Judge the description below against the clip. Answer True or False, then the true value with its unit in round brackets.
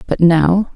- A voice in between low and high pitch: True (175 Hz)